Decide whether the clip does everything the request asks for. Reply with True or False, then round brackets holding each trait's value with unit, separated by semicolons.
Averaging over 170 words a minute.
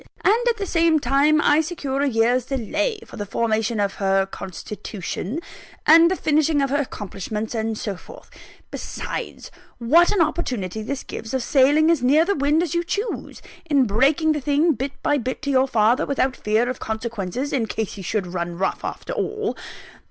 True (185 wpm)